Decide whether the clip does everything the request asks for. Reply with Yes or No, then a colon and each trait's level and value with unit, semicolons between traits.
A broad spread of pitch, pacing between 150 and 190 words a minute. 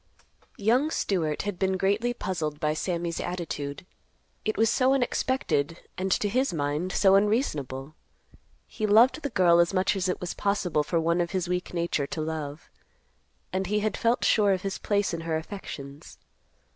No: average, 4.4 semitones; average, 170 wpm